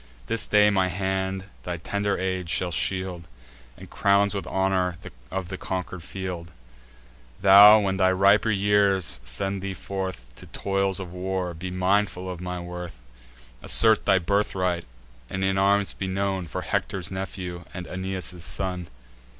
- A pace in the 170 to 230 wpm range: No, average, 150 wpm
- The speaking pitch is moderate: No, very low, 95 Hz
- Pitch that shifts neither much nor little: No, narrow, 1.4 semitones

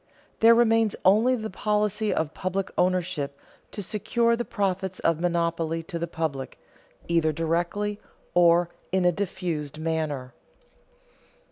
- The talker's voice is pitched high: No, medium, 180 Hz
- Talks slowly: Yes, slow, 125 wpm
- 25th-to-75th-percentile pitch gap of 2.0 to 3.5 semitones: No, average, 4.0 semitones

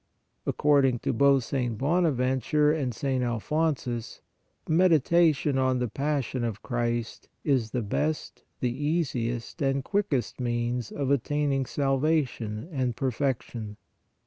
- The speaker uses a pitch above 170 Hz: No, low, 135 Hz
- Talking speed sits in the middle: No, slow, 120 wpm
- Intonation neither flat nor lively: Yes, average, 3.6 semitones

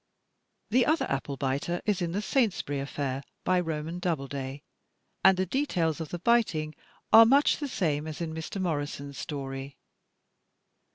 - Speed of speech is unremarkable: Yes, average, 150 wpm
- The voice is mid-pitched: Yes, medium, 160 Hz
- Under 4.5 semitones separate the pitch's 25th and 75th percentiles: No, average, 5.1 semitones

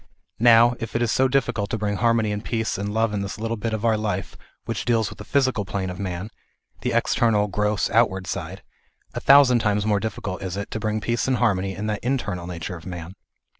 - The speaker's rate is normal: No, fast, 220 wpm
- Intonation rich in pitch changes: No, average, 2.8 semitones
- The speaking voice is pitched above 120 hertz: No, low, 105 Hz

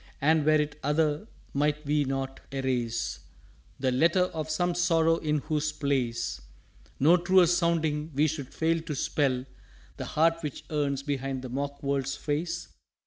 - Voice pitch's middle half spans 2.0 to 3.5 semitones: Yes, average, 2.9 semitones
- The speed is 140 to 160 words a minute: Yes, average, 155 wpm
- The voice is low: No, medium, 150 Hz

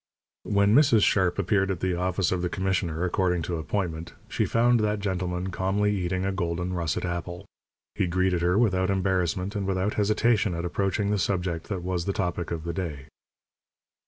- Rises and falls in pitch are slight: Yes, narrow, 2.3 semitones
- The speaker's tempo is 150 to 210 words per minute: Yes, average, 180 wpm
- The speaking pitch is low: Yes, very low, 95 Hz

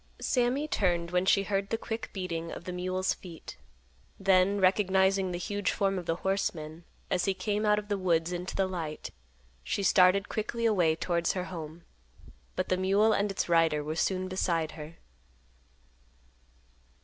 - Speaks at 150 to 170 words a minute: Yes, average, 165 wpm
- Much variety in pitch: No, average, 2.7 semitones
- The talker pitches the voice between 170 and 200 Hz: Yes, medium, 185 Hz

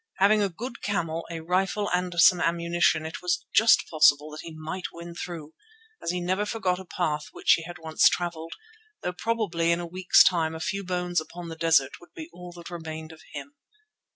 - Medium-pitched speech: Yes, medium, 175 Hz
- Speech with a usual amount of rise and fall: No, narrow, 2.1 semitones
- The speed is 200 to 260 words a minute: Yes, fast, 205 wpm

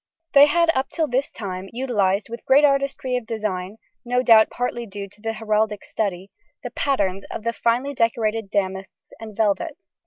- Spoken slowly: No, average, 175 wpm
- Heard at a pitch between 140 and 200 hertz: No, high, 225 Hz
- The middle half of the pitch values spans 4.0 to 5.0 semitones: Yes, average, 4.3 semitones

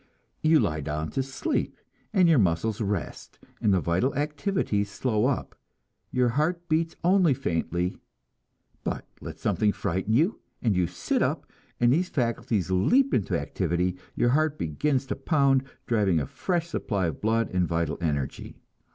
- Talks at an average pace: Yes, average, 155 wpm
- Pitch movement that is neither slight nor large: No, wide, 8.8 semitones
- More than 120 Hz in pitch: No, low, 115 Hz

